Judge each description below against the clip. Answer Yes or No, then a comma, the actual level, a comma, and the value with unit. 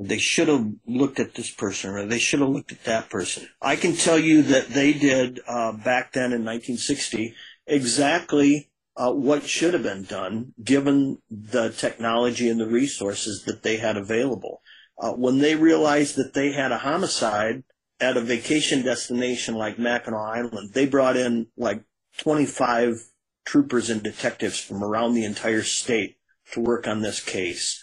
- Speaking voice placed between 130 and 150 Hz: No, low, 120 Hz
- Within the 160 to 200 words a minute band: Yes, average, 170 wpm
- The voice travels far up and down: No, average, 3.9 semitones